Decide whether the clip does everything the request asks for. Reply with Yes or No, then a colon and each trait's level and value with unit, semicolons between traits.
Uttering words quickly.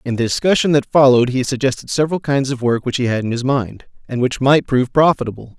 Yes: fast, 235 wpm